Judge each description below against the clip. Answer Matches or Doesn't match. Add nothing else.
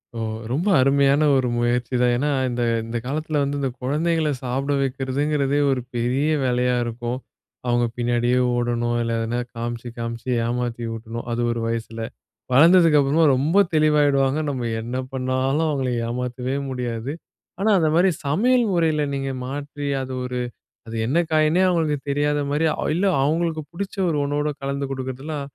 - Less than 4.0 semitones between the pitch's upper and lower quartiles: Matches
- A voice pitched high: Doesn't match